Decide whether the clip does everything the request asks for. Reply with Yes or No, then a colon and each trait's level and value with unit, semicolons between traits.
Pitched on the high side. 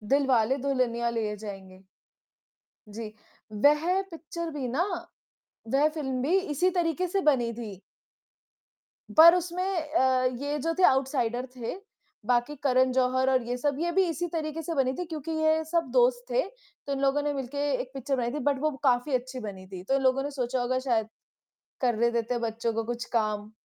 Yes: very high, 260 Hz